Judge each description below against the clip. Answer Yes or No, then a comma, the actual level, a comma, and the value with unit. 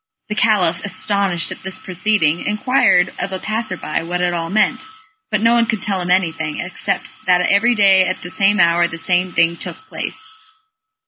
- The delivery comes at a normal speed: Yes, average, 190 wpm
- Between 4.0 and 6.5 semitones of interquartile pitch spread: No, average, 3.3 semitones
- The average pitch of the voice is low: No, medium, 185 Hz